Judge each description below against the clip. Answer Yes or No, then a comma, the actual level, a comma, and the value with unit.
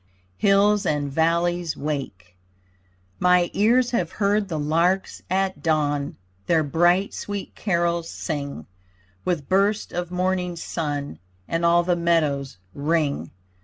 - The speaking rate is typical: No, slow, 120 wpm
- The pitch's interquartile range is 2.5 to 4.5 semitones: Yes, average, 3.6 semitones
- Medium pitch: Yes, medium, 170 Hz